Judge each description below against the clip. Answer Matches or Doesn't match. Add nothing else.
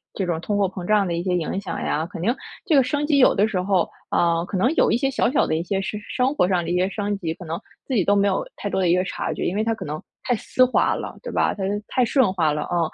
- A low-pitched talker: Doesn't match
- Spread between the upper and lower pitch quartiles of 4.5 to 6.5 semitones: Matches